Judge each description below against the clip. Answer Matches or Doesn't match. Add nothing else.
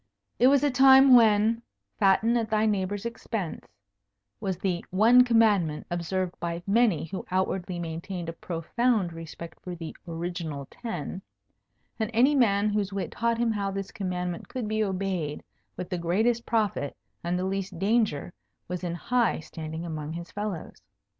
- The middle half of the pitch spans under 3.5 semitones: Doesn't match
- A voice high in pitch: Matches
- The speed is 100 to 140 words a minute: Doesn't match